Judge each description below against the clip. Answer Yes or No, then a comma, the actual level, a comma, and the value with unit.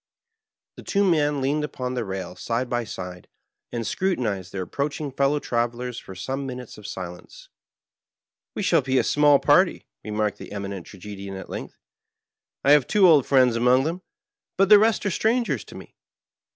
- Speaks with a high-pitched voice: No, low, 130 Hz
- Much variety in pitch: Yes, wide, 6.0 semitones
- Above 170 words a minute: Yes, average, 180 wpm